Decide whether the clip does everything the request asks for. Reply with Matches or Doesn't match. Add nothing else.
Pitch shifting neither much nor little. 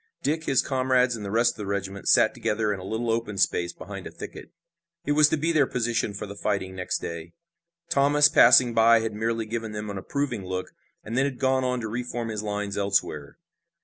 Matches